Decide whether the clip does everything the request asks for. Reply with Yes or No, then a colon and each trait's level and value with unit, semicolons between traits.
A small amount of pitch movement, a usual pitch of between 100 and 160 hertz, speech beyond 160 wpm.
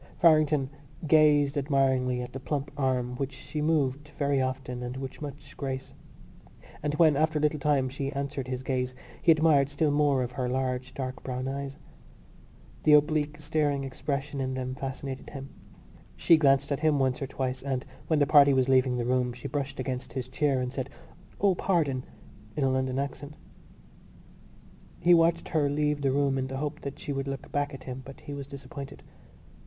Yes: narrow, 2.0 semitones; medium, 140 Hz; average, 185 wpm